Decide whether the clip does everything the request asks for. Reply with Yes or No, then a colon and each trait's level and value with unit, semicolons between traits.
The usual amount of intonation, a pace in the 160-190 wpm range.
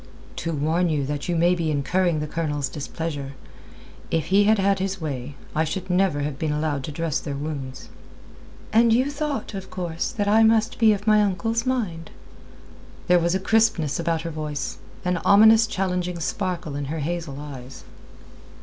Yes: average, 4.9 semitones; average, 175 wpm